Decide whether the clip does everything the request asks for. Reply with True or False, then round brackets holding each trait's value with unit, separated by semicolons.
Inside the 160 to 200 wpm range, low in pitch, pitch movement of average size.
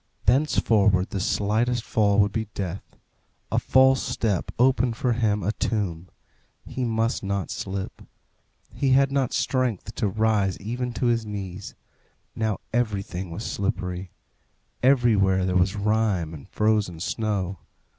False (135 wpm; 105 Hz; 3.6 semitones)